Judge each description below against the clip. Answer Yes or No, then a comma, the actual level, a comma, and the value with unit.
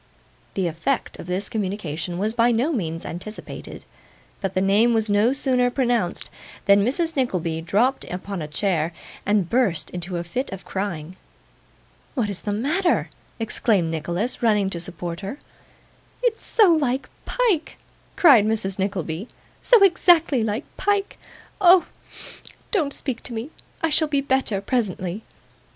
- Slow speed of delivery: No, average, 145 wpm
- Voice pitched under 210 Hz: No, high, 215 Hz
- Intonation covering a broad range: Yes, wide, 6.5 semitones